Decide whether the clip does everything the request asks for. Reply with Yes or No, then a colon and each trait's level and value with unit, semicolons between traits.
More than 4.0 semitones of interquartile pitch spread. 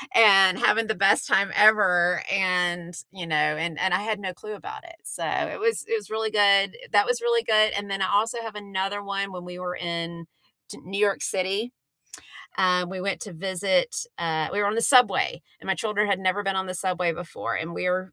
No: average, 2.9 semitones